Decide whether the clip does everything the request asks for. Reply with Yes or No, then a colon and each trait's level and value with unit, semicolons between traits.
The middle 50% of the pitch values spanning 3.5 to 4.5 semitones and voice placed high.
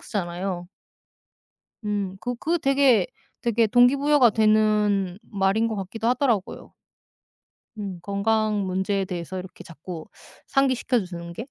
Yes: average, 3.9 semitones; high, 205 Hz